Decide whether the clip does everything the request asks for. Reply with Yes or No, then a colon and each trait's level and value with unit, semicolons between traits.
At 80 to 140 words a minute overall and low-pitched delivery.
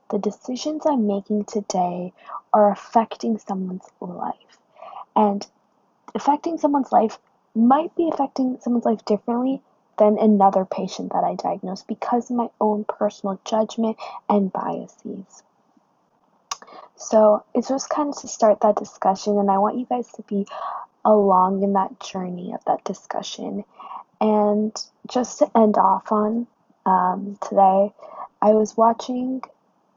No: slow, 135 wpm; high, 215 Hz